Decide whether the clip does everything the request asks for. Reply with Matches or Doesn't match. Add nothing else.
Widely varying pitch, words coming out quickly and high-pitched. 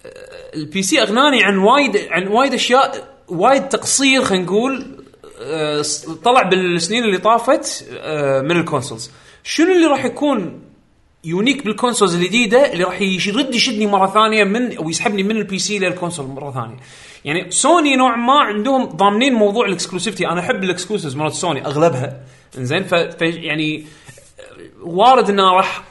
Matches